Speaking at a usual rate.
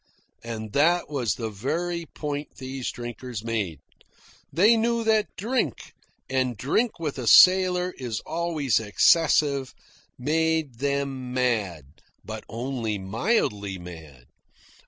No: slow, 115 wpm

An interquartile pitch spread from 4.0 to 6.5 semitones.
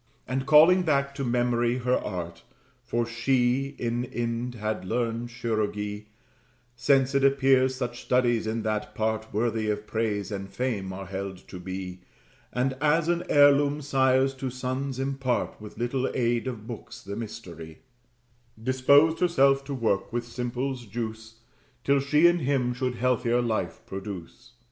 No: average, 3.5 semitones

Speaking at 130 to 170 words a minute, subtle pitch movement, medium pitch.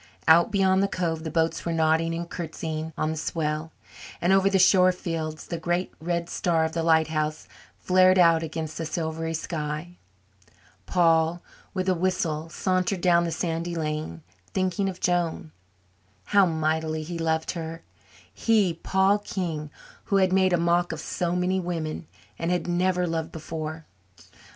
Yes: average, 160 wpm; narrow, 2.1 semitones; medium, 165 Hz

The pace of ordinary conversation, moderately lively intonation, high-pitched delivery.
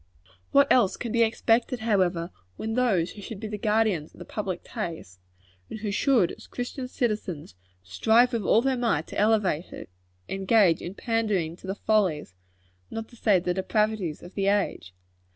Yes: average, 175 wpm; average, 4.0 semitones; high, 210 Hz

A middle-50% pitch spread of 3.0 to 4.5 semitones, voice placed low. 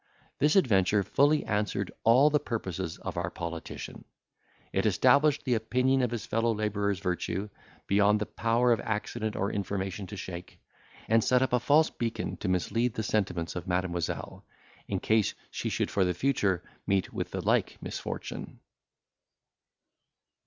Yes: average, 4.1 semitones; low, 105 Hz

